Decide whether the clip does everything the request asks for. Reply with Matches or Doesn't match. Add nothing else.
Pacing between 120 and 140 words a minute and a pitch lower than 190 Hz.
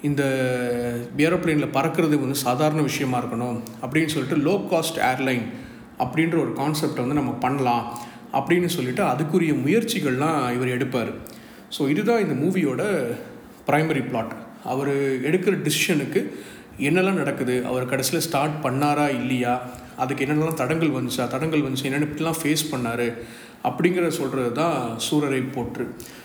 Matches